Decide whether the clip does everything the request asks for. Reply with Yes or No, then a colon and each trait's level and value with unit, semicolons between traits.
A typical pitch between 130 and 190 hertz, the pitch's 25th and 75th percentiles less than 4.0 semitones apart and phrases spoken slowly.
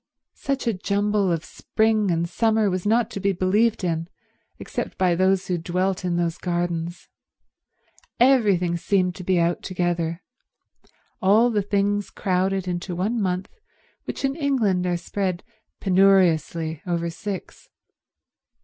Yes: medium, 185 Hz; average, 2.9 semitones; slow, 130 wpm